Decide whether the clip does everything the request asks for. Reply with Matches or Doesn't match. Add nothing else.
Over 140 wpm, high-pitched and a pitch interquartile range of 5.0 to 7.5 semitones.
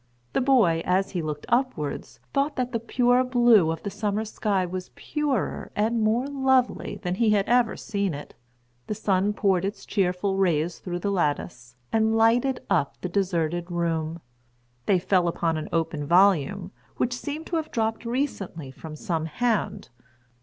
Matches